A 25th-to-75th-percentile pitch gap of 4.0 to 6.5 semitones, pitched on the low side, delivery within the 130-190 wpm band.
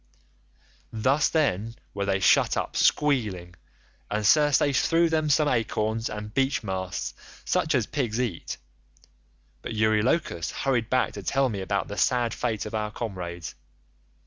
Yes: average, 4.9 semitones; low, 110 Hz; average, 145 wpm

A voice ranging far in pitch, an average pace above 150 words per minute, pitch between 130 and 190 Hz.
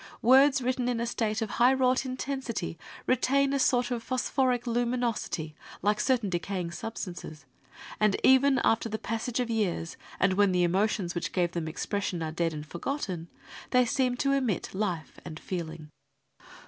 No: wide, 6.2 semitones; average, 165 wpm; high, 225 Hz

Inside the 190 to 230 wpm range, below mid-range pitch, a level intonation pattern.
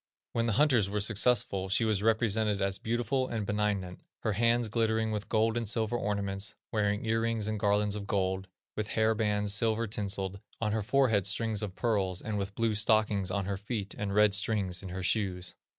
Yes: average, 195 wpm; low, 105 Hz; narrow, 2.1 semitones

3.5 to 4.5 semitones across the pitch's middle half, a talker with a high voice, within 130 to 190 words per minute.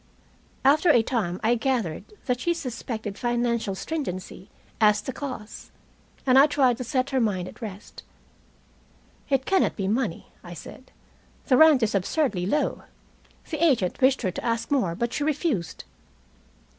No: average, 4.9 semitones; high, 240 Hz; average, 155 wpm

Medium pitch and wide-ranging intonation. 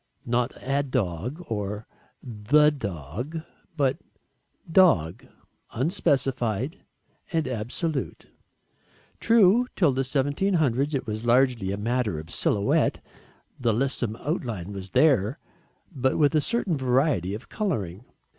No: low, 130 Hz; wide, 6.0 semitones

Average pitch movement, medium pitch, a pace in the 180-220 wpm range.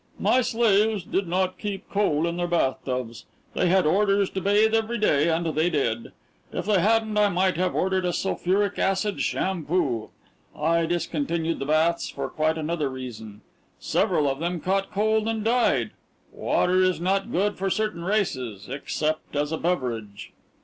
No: average, 4.5 semitones; medium, 180 Hz; average, 165 wpm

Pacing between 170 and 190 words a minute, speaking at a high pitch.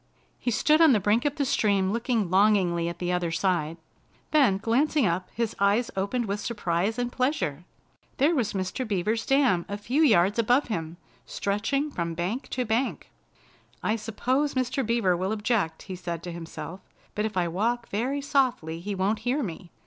Yes: average, 180 wpm; high, 210 Hz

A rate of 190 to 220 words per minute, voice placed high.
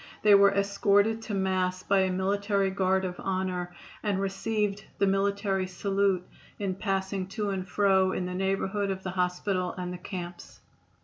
No: average, 165 wpm; high, 195 Hz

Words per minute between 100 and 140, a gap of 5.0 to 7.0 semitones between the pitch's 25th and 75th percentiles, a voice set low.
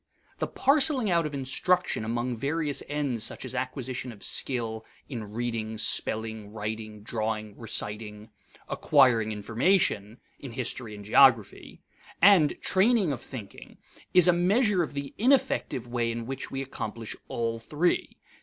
Yes: slow, 135 wpm; average, 5.3 semitones; low, 125 Hz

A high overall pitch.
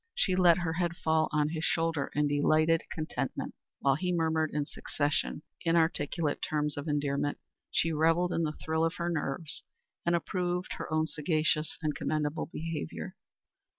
No: medium, 160 Hz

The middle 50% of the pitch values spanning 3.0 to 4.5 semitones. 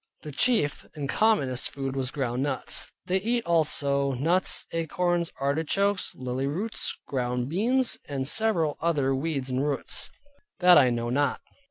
No: average, 5.1 semitones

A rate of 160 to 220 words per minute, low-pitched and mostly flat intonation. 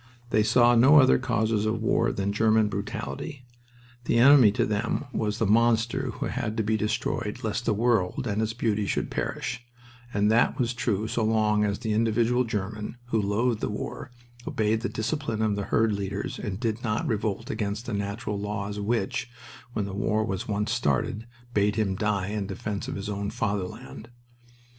Yes: average, 180 wpm; low, 110 Hz; narrow, 2.1 semitones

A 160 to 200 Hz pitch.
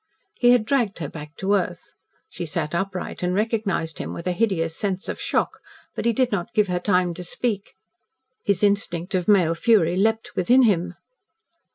Yes: high, 190 Hz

